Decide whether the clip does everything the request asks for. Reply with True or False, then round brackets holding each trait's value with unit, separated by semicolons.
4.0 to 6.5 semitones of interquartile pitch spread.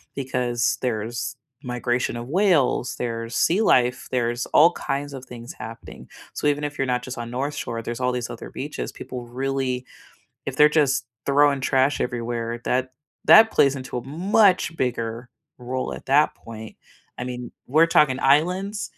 False (3.1 semitones)